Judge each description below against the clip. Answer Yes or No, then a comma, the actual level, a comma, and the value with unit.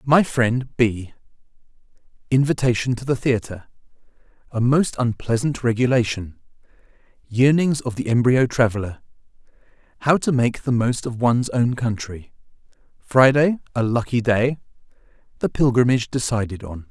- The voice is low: Yes, low, 120 Hz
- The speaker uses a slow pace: Yes, slow, 95 wpm